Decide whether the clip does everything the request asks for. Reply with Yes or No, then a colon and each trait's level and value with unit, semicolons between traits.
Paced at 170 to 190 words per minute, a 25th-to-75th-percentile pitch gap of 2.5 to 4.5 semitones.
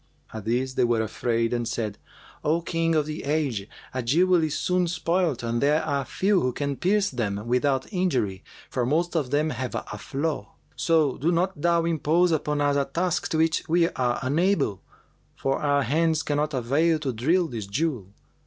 No: average, 185 wpm; average, 4.9 semitones